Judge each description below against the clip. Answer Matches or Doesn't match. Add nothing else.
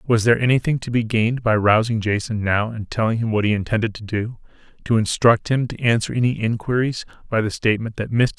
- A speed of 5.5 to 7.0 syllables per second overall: Matches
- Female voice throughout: Doesn't match